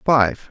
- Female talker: No, male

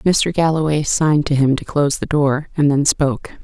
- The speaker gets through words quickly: Yes, fast, 210 wpm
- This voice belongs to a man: No, female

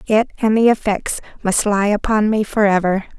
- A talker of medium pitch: No, high, 210 Hz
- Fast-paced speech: No, average, 170 wpm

